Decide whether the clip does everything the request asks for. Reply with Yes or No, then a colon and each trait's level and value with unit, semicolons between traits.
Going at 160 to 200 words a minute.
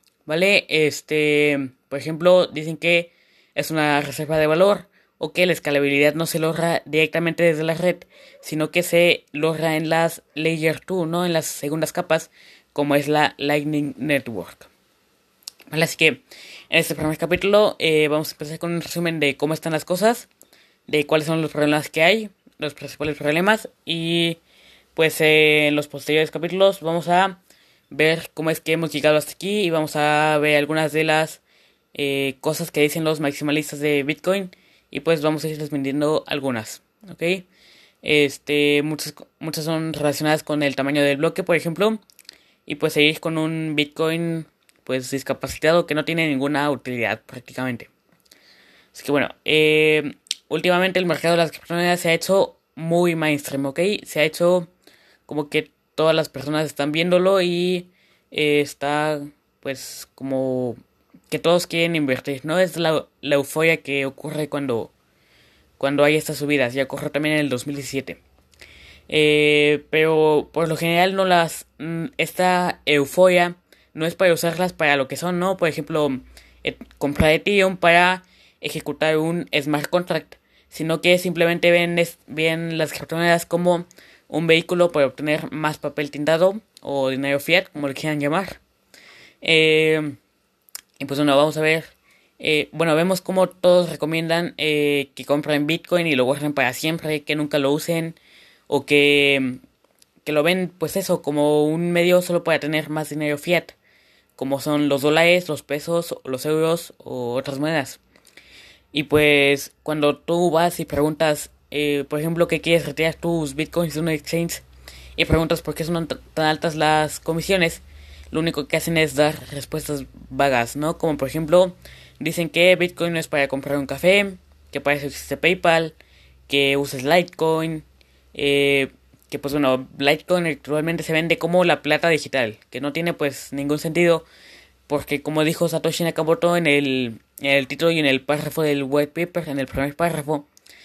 Yes: average, 165 wpm